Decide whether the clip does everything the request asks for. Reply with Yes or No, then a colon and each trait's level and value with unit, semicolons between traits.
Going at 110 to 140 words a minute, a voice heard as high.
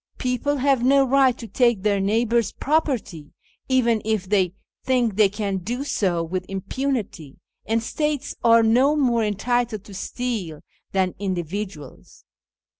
Yes: slow, 135 wpm; high, 225 Hz